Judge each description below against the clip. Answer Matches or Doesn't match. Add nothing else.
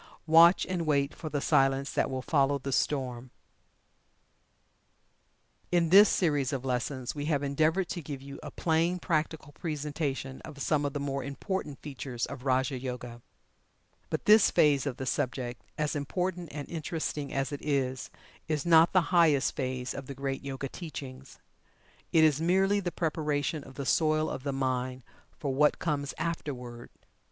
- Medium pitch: Matches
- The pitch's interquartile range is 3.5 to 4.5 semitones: Doesn't match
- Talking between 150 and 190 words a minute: Matches